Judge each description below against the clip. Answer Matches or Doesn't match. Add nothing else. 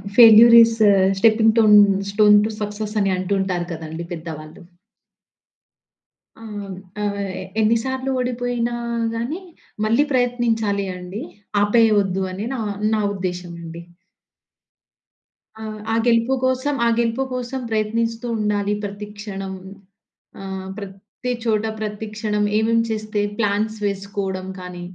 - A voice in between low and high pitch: Doesn't match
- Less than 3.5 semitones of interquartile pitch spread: Matches